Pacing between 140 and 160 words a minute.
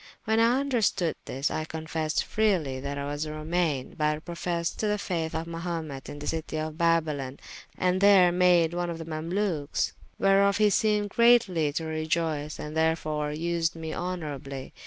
No: average, 170 wpm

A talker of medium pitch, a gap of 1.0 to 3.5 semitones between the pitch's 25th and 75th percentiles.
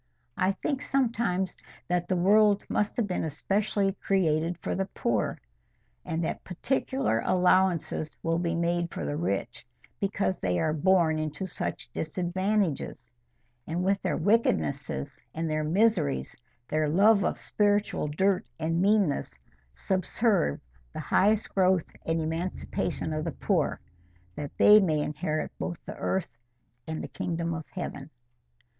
No: medium, 175 Hz; average, 3.9 semitones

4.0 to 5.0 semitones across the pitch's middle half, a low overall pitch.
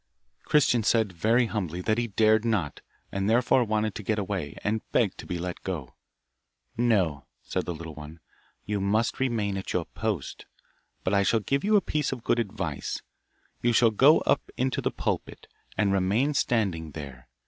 Yes: average, 4.5 semitones; low, 105 Hz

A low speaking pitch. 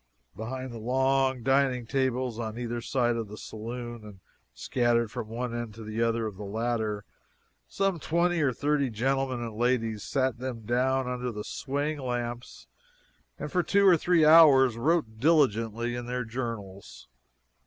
Yes: low, 120 Hz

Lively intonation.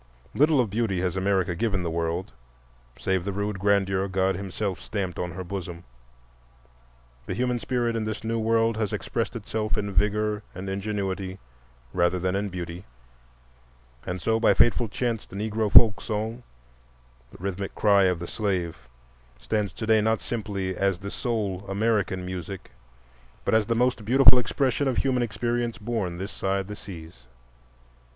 No: average, 3.4 semitones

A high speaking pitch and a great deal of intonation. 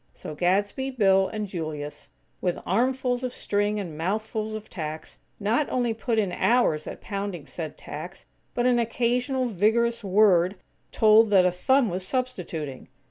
No: high, 205 Hz; average, 4.7 semitones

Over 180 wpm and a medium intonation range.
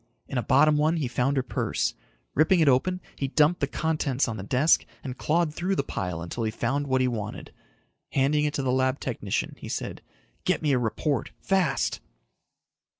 Yes: average, 195 wpm; average, 3.5 semitones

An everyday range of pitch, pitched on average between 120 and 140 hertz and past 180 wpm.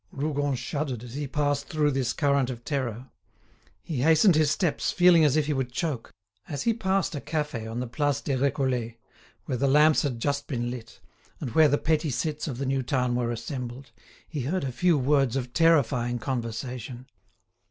Yes: average, 3.4 semitones; low, 135 Hz; average, 190 wpm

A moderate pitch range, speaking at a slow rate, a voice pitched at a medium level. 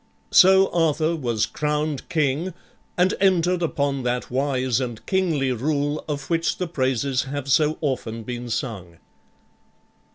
Yes: average, 4.4 semitones; slow, 130 wpm; medium, 145 Hz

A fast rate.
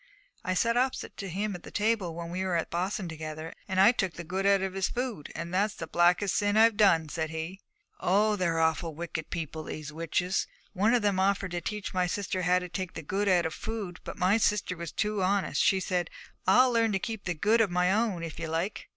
Yes: fast, 235 wpm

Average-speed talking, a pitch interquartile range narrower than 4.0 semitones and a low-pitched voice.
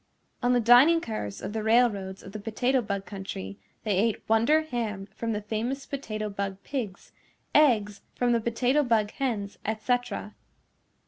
No: average, 160 wpm; average, 3.3 semitones; high, 225 Hz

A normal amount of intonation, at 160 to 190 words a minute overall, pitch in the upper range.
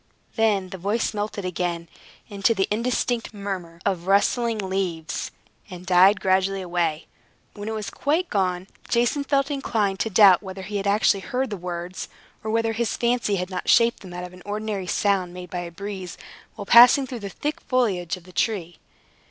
Yes: average, 3.5 semitones; average, 185 wpm; high, 200 Hz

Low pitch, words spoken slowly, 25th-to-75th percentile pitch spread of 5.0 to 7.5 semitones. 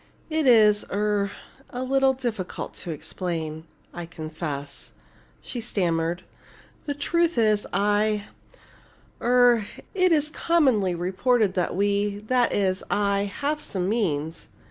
No: high, 205 Hz; slow, 120 wpm; wide, 5.5 semitones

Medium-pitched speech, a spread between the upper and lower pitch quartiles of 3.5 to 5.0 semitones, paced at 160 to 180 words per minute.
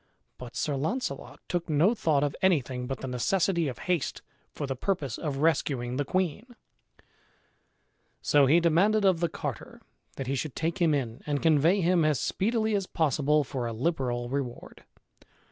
Yes: medium, 150 Hz; average, 4.6 semitones; average, 165 wpm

